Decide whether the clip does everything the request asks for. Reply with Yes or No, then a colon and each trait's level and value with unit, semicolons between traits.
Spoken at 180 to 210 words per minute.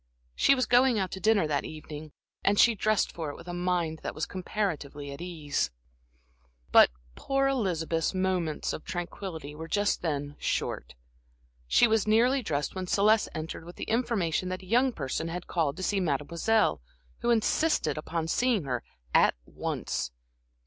No: average, 165 wpm